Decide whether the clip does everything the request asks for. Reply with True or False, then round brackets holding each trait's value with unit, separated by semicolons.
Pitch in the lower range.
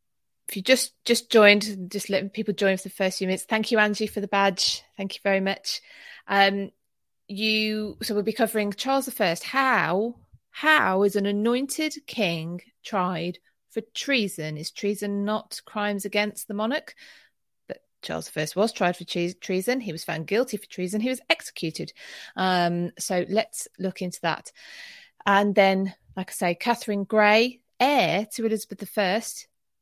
False (205 Hz)